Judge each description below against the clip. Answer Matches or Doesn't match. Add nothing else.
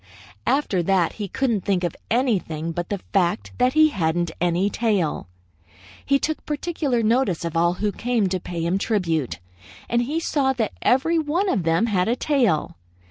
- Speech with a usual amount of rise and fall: Doesn't match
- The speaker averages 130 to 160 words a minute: Doesn't match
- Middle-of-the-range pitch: Doesn't match